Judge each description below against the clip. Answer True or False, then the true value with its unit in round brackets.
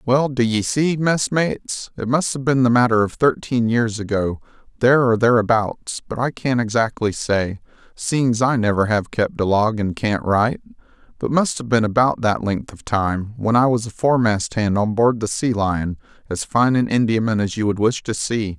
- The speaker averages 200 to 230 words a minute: True (205 wpm)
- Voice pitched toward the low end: True (115 Hz)